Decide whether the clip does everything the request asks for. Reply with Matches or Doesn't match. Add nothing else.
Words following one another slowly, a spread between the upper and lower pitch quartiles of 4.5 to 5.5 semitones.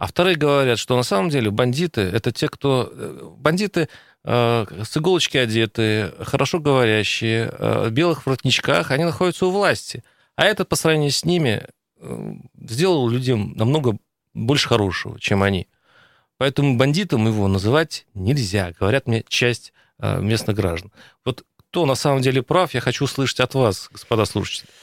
Doesn't match